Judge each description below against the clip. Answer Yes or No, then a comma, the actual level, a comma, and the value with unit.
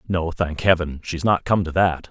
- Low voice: Yes, very low, 85 Hz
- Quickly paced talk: Yes, fast, 230 wpm